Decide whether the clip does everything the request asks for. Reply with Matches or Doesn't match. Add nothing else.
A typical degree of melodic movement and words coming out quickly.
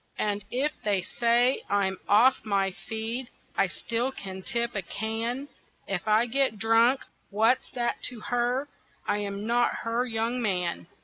Doesn't match